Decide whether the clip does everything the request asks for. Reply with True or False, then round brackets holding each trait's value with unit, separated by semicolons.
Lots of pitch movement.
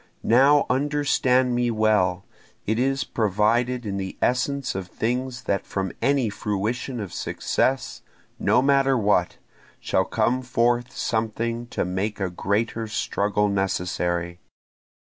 False (4.1 semitones)